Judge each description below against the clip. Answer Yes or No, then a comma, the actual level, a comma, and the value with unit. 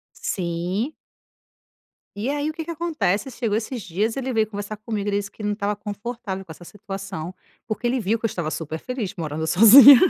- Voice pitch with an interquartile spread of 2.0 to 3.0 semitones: No, average, 4.1 semitones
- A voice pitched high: Yes, high, 210 Hz